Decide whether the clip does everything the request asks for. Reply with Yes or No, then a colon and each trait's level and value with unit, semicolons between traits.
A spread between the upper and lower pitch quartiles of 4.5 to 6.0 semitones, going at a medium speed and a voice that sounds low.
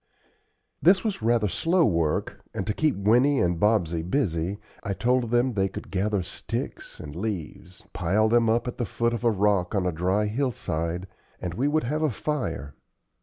Yes: wide, 5.4 semitones; average, 180 wpm; low, 105 Hz